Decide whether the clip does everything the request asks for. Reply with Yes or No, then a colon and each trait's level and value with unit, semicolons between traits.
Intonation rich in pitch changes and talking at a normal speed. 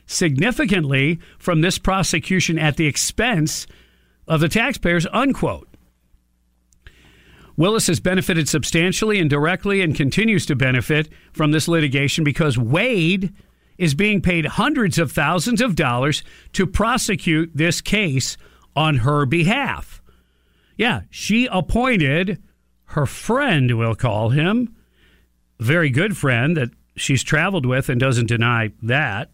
No: wide, 6.5 semitones; slow, 125 wpm